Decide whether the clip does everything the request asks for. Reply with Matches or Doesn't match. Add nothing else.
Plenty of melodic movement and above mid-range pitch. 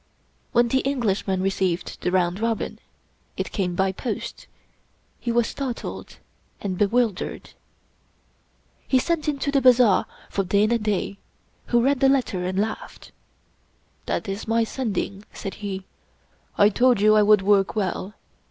Doesn't match